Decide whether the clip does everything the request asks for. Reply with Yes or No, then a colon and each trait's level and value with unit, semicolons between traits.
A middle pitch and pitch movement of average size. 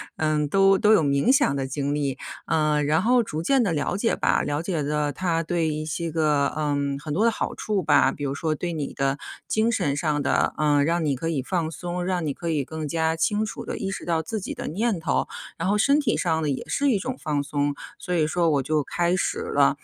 Yes: medium, 160 Hz; average, 4.1 semitones